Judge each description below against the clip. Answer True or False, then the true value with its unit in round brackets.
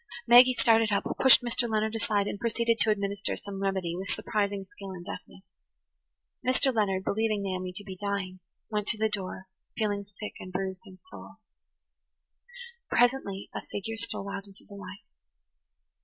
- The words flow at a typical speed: True (160 wpm)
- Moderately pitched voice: False (200 Hz)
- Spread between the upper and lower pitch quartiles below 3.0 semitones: True (2.5 semitones)